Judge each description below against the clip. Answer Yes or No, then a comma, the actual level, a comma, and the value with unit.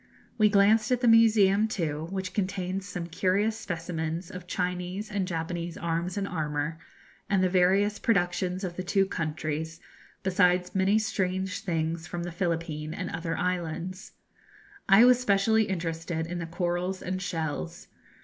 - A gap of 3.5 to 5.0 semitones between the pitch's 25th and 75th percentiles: No, average, 2.9 semitones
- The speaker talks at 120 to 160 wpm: Yes, average, 150 wpm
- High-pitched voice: No, medium, 180 Hz